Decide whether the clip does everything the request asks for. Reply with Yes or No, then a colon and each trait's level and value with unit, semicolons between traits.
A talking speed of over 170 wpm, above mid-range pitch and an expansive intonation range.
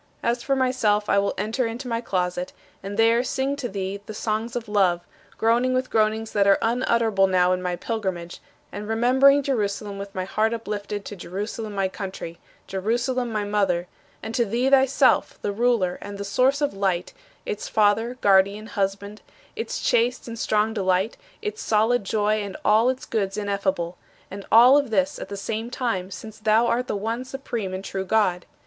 No: average, 180 wpm; high, 215 Hz; average, 3.2 semitones